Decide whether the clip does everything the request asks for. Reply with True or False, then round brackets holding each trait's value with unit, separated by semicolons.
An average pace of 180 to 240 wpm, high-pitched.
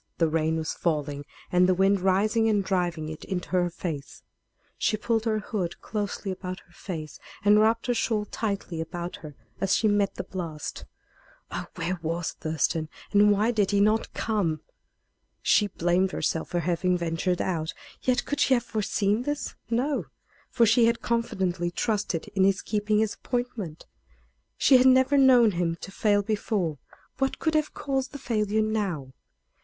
False (170 wpm; 200 Hz)